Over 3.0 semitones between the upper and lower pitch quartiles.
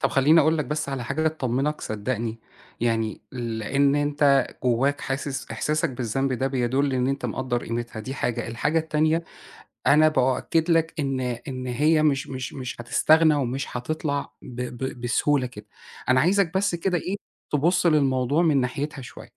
Yes: average, 3.6 semitones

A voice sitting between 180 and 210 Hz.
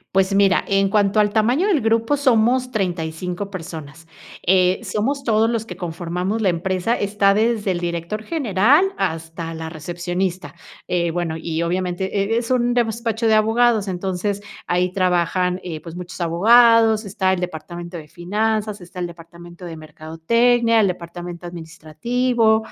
Yes: high, 190 Hz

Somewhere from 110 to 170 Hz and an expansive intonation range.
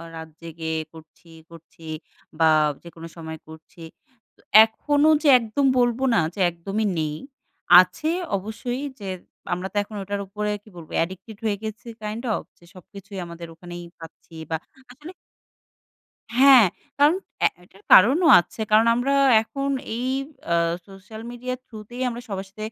No: high, 205 Hz; wide, 6.0 semitones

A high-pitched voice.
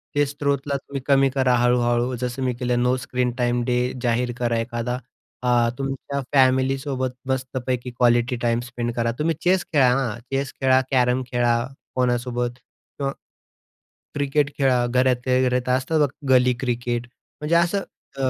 No: low, 125 Hz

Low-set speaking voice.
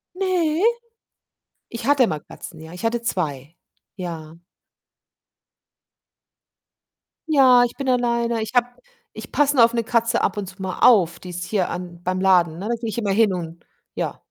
No: high, 215 Hz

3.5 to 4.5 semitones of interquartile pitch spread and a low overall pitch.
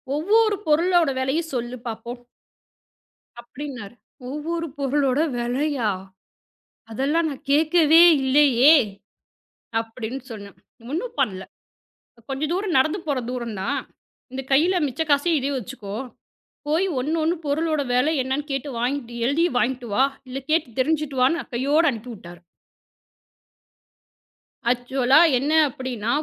No: average, 4.0 semitones; very high, 270 Hz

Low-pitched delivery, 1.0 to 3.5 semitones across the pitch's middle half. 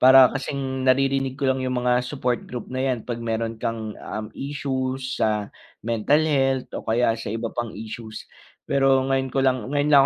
Yes: low, 130 Hz; average, 2.7 semitones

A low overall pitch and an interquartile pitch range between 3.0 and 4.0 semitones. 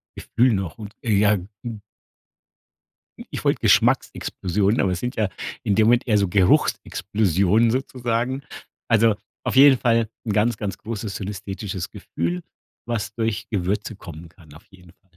Yes: low, 105 Hz; average, 3.3 semitones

